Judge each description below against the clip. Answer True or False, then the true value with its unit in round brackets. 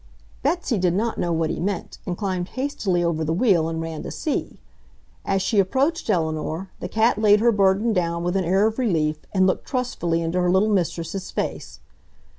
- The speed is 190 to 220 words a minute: True (195 wpm)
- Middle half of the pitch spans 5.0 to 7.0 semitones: False (4.1 semitones)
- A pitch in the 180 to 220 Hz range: True (185 Hz)